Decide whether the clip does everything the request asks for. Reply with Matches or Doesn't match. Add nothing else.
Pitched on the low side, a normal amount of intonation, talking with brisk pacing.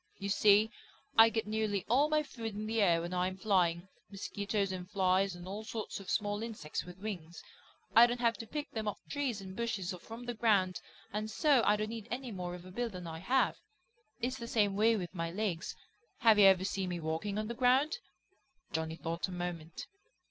Doesn't match